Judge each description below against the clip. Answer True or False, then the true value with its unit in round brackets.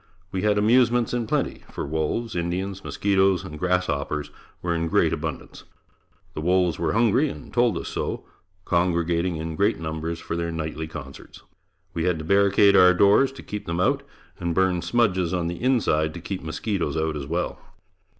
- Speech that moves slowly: False (175 wpm)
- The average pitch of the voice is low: True (90 Hz)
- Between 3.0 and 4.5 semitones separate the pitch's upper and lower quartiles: True (3.6 semitones)